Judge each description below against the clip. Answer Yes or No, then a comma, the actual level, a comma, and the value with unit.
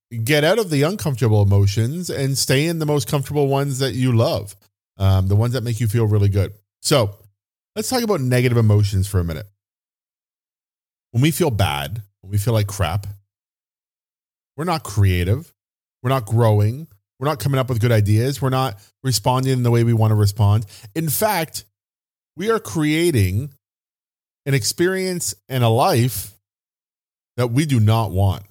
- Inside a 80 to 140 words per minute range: No, average, 170 wpm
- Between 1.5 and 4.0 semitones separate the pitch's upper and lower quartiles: No, average, 5.2 semitones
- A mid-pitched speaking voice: No, low, 115 Hz